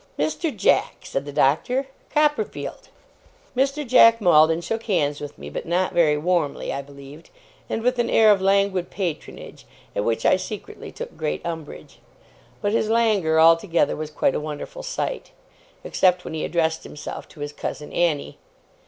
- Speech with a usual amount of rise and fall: No, wide, 6.9 semitones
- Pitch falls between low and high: Yes, medium, 175 Hz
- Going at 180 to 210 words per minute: No, average, 160 wpm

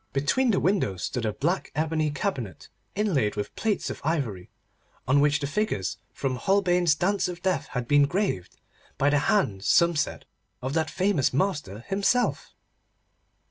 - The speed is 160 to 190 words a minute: No, average, 150 wpm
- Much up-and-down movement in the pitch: Yes, wide, 6.4 semitones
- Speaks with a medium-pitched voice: Yes, medium, 150 Hz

